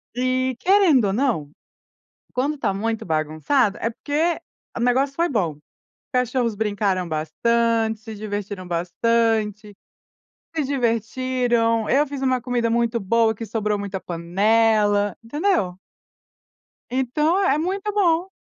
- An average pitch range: Yes, average, 4.2 semitones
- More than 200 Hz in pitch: Yes, high, 230 Hz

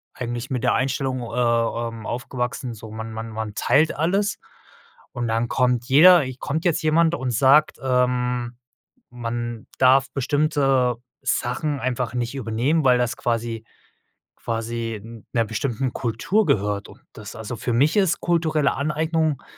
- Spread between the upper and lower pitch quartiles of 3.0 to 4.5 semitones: Yes, average, 3.5 semitones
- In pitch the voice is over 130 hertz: No, low, 125 Hz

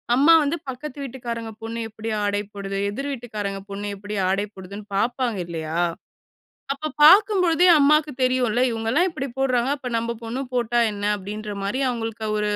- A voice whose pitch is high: Yes, high, 230 Hz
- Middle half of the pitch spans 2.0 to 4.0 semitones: No, average, 4.6 semitones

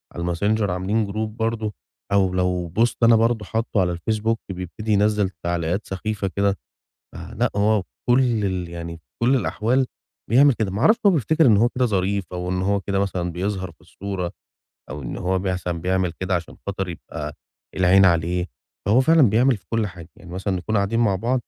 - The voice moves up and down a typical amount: Yes, average, 3.6 semitones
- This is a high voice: No, low, 100 Hz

